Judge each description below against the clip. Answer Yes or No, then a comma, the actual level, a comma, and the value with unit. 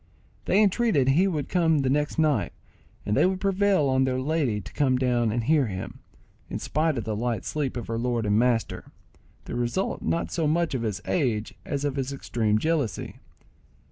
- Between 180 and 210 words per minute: Yes, average, 190 wpm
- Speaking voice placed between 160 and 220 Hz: No, low, 135 Hz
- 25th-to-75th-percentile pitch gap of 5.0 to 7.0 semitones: Yes, average, 5.3 semitones